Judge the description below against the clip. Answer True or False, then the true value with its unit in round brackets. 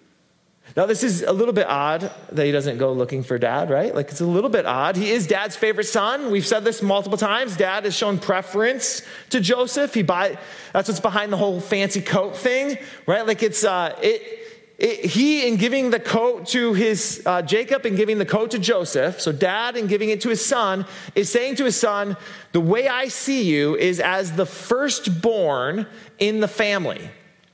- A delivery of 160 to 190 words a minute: False (205 wpm)